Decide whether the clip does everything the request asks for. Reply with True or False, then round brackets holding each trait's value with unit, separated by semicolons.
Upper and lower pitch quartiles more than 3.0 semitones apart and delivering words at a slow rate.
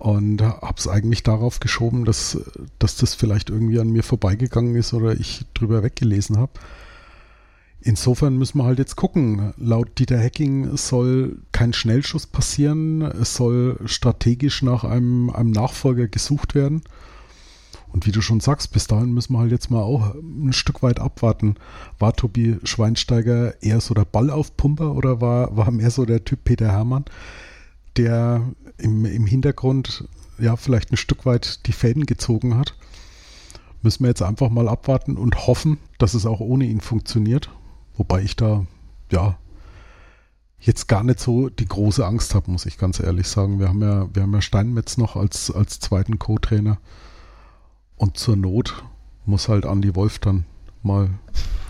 False (3.4 semitones; 165 wpm)